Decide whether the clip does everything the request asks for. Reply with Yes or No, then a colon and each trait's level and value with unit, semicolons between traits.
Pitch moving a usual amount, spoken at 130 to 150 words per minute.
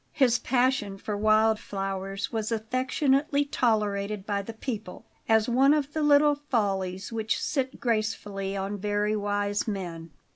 Yes: average, 4.2 semitones; average, 140 wpm